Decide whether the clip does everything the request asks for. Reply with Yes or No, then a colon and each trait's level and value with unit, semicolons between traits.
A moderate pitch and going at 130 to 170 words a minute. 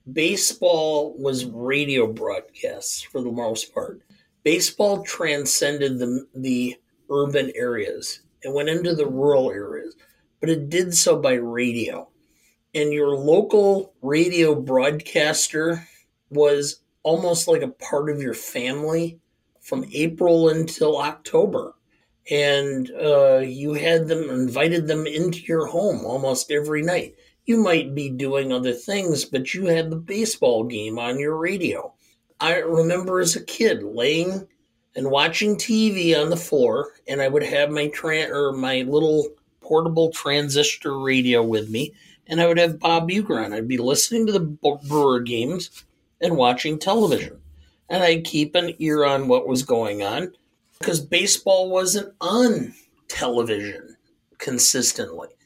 Yes: medium, 155 Hz; average, 140 wpm